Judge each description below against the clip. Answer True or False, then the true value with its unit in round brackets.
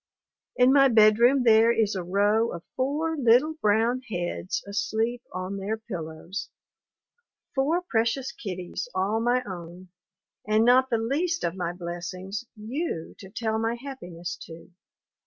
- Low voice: False (220 Hz)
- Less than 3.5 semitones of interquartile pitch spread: False (5.1 semitones)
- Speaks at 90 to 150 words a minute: True (140 wpm)